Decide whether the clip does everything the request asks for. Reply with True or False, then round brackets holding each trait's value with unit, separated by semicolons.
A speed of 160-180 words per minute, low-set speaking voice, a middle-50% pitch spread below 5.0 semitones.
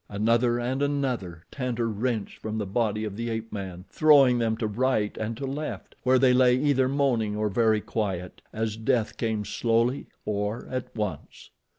True (175 wpm; 115 Hz; 3.2 semitones)